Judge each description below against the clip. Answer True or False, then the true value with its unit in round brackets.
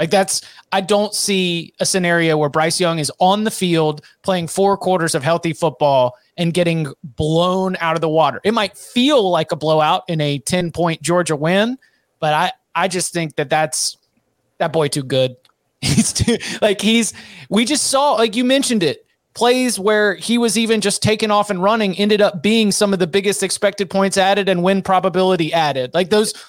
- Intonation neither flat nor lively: True (4.0 semitones)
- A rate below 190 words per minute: False (195 wpm)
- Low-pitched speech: False (185 Hz)